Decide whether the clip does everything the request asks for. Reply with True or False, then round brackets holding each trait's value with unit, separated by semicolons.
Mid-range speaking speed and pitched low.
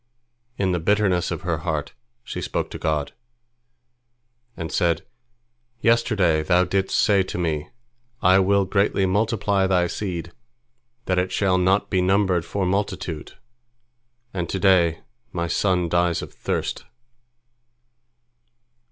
False (125 wpm; 90 Hz)